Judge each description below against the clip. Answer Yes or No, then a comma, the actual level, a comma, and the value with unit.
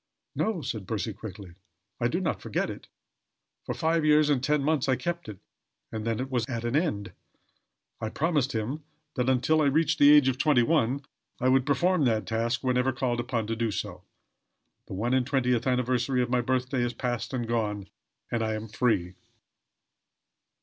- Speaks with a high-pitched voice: No, low, 125 Hz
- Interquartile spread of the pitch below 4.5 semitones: Yes, average, 3.6 semitones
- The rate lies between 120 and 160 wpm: No, average, 185 wpm